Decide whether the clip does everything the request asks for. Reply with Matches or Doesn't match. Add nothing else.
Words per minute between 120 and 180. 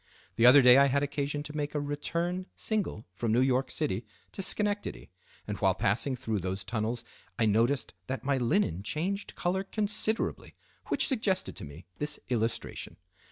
Matches